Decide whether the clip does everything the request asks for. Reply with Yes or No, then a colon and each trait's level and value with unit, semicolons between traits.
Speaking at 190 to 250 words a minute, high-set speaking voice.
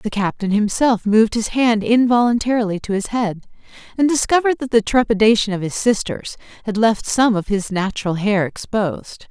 No: average, 170 wpm; high, 220 Hz